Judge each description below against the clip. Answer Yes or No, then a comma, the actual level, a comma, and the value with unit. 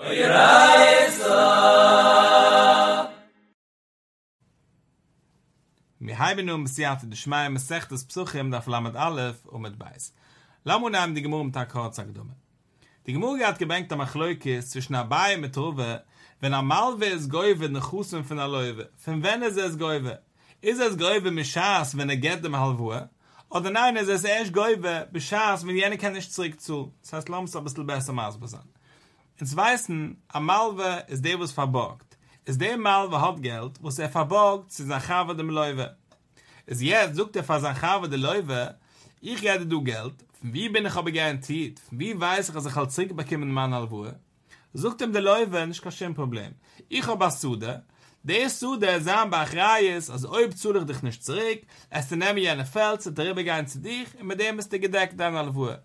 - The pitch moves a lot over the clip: Yes, wide, 6.0 semitones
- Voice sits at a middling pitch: Yes, medium, 155 Hz